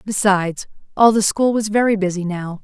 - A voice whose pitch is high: Yes, high, 200 Hz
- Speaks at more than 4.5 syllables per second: Yes, 5.3 syllables/s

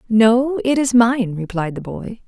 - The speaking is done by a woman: Yes, female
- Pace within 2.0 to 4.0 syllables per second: Yes, 3.9 syllables/s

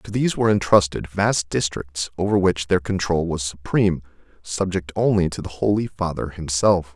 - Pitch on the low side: Yes, very low, 90 Hz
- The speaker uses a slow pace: No, average, 165 wpm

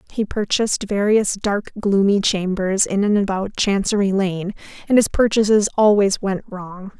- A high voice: Yes, high, 200 Hz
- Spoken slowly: No, average, 145 wpm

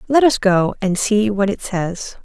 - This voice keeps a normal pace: No, fast, 215 wpm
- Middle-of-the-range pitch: No, high, 205 Hz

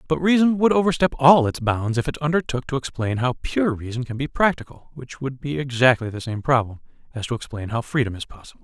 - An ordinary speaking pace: No, fast, 220 wpm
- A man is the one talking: Yes, male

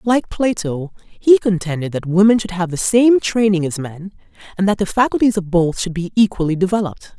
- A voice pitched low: No, high, 190 Hz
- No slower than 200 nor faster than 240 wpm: No, average, 190 wpm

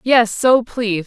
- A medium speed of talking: Yes, average, 170 wpm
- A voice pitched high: Yes, high, 230 Hz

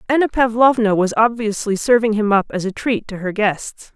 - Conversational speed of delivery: Yes, average, 195 wpm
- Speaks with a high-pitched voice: Yes, high, 215 Hz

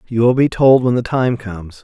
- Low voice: Yes, low, 120 Hz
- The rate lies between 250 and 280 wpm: Yes, fast, 260 wpm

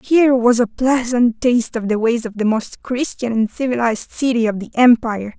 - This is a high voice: Yes, high, 235 Hz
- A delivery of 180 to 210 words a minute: Yes, average, 200 wpm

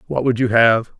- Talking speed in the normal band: No, fast, 240 wpm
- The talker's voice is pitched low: Yes, low, 120 Hz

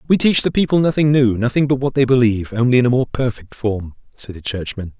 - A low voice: Yes, low, 125 Hz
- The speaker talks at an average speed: No, fast, 240 wpm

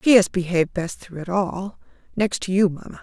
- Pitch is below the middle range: No, high, 190 Hz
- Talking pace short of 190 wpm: No, average, 200 wpm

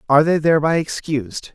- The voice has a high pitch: No, medium, 150 Hz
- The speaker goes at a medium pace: Yes, average, 155 wpm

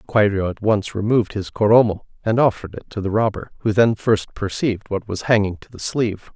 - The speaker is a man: Yes, male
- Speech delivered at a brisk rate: Yes, fast, 210 wpm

